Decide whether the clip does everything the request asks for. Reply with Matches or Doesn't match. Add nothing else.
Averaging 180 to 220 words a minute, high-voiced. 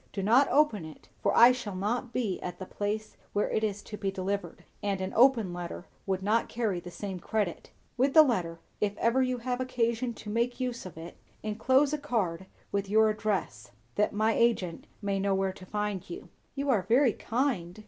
Matches